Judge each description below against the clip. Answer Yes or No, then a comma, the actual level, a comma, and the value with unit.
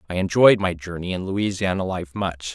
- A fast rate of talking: No, average, 190 wpm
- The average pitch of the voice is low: Yes, very low, 90 Hz